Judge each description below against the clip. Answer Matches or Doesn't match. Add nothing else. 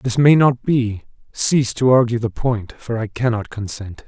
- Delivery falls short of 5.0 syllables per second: Matches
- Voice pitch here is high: Doesn't match